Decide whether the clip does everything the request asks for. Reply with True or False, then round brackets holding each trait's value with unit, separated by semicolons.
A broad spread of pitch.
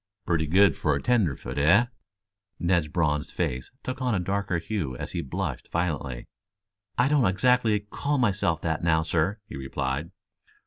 True (5.7 semitones)